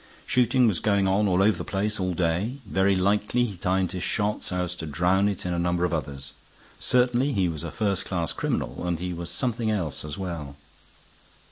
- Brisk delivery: Yes, fast, 210 wpm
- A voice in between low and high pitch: No, very low, 95 Hz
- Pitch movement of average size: Yes, average, 3.3 semitones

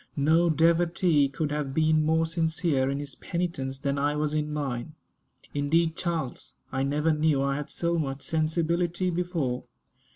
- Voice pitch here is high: No, medium, 155 Hz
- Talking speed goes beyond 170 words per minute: No, average, 155 wpm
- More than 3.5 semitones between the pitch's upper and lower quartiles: No, average, 2.9 semitones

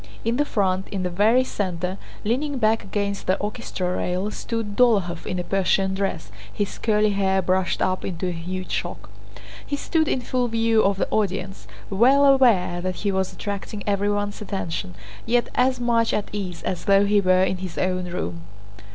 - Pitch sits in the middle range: No, high, 200 Hz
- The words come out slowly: No, average, 180 wpm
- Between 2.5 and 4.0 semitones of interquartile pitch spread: Yes, average, 3.4 semitones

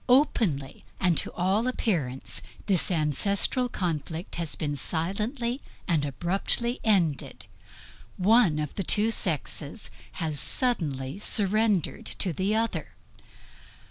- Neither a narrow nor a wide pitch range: No, wide, 6.2 semitones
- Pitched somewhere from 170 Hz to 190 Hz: Yes, medium, 185 Hz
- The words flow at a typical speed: No, slow, 105 wpm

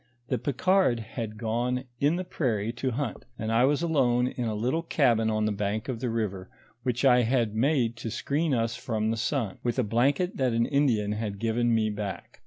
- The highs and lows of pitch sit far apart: No, average, 3.2 semitones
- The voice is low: Yes, low, 120 Hz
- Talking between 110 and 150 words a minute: No, fast, 205 wpm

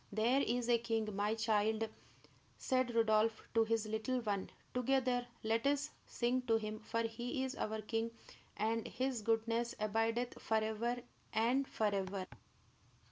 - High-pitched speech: Yes, high, 225 Hz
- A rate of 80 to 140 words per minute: Yes, slow, 135 wpm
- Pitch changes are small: Yes, narrow, 2.0 semitones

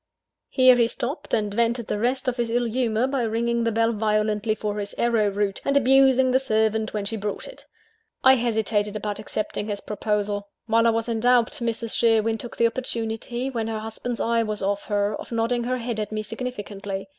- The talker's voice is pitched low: No, high, 225 Hz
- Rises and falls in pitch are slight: Yes, narrow, 2.2 semitones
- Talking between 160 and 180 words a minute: No, fast, 205 wpm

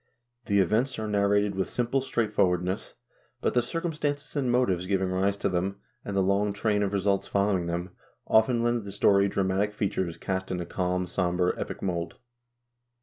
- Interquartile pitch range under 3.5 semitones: Yes, average, 2.9 semitones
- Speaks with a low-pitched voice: Yes, low, 100 Hz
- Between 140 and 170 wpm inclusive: No, average, 185 wpm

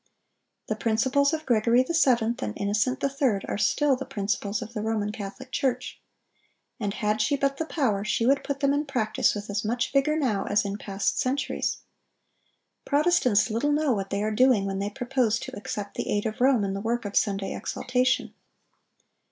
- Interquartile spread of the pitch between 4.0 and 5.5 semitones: Yes, average, 4.6 semitones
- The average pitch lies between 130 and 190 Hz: No, high, 230 Hz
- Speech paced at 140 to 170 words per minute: No, average, 185 wpm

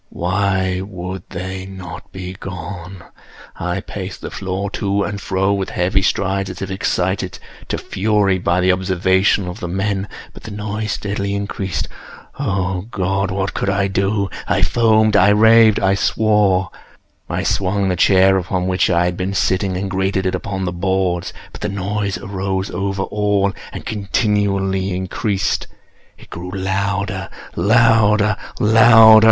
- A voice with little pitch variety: Yes, narrow, 1.5 semitones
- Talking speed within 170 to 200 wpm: No, average, 140 wpm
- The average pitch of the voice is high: No, very low, 95 Hz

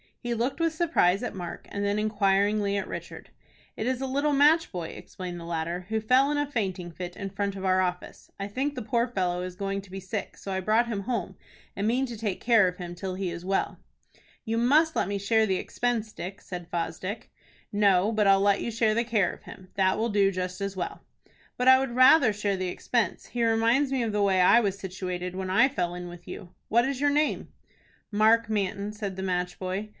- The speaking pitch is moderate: No, high, 200 Hz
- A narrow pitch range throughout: No, average, 4.0 semitones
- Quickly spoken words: Yes, fast, 230 wpm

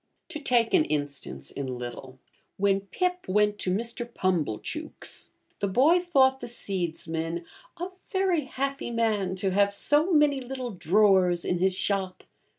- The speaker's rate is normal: Yes, average, 145 wpm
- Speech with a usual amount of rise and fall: No, wide, 6.8 semitones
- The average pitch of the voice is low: No, high, 200 Hz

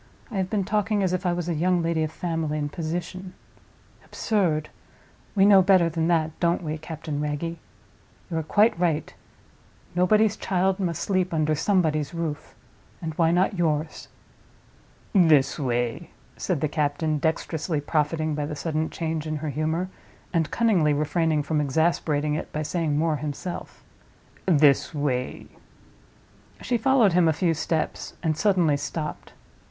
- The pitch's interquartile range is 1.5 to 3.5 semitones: Yes, average, 2.9 semitones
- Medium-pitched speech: Yes, medium, 160 Hz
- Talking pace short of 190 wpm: Yes, average, 150 wpm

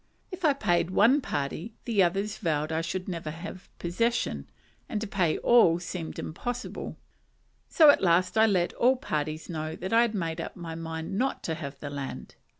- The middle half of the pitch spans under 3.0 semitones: No, wide, 5.4 semitones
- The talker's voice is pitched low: No, medium, 175 Hz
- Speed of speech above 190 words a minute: No, average, 185 wpm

